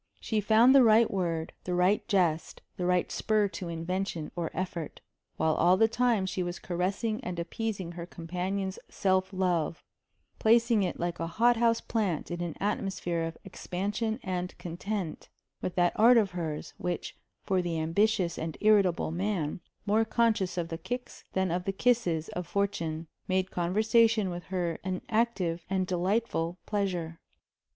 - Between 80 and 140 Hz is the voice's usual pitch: No, medium, 185 Hz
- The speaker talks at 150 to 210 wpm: Yes, average, 160 wpm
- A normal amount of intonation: Yes, average, 3.7 semitones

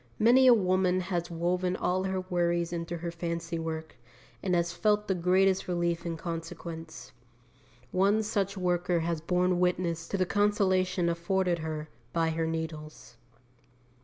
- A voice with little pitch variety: Yes, narrow, 1.9 semitones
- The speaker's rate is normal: Yes, average, 145 wpm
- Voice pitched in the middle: Yes, medium, 175 Hz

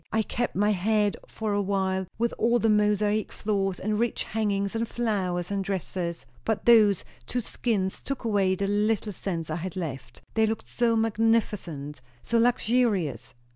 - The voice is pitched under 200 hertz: No, high, 205 Hz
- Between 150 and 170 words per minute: Yes, average, 165 wpm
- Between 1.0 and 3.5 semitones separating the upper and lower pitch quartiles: Yes, average, 3.0 semitones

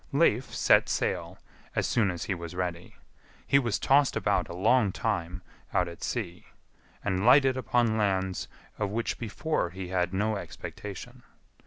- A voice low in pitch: Yes, low, 100 Hz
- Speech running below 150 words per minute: No, average, 155 wpm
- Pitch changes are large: No, average, 4.5 semitones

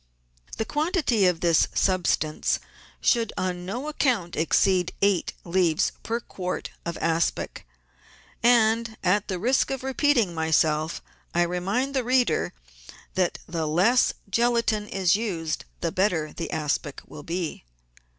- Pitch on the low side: No, medium, 185 Hz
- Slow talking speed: Yes, slow, 130 wpm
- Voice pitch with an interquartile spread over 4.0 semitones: Yes, wide, 5.6 semitones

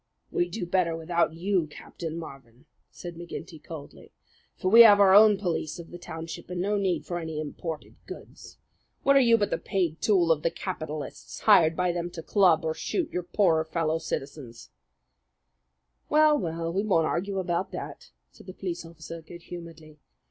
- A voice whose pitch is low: No, medium, 170 Hz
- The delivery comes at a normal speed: Yes, average, 175 wpm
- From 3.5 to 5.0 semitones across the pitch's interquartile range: No, average, 2.9 semitones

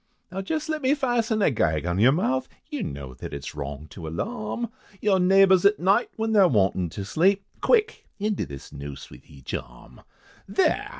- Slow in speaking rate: No, average, 185 wpm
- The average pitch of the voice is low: No, medium, 180 Hz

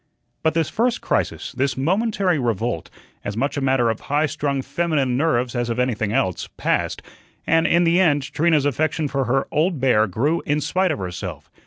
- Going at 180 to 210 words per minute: Yes, average, 185 wpm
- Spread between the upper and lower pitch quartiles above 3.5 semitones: Yes, average, 5.0 semitones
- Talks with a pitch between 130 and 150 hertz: Yes, medium, 140 Hz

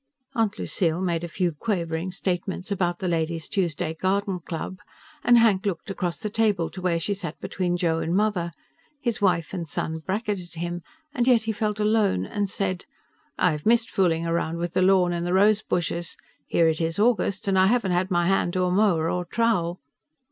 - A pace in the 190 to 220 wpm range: Yes, average, 195 wpm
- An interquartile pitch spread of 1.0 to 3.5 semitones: Yes, average, 3.2 semitones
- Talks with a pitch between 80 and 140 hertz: No, medium, 185 Hz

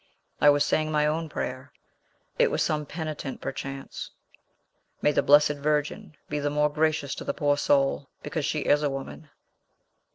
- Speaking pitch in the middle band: Yes, medium, 150 Hz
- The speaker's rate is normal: Yes, average, 165 wpm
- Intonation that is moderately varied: No, narrow, 1.2 semitones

